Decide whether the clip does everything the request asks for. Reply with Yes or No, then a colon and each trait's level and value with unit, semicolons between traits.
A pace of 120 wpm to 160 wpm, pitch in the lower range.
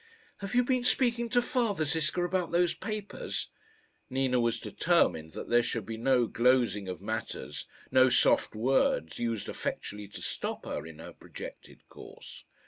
Yes: average, 155 wpm; low, 130 Hz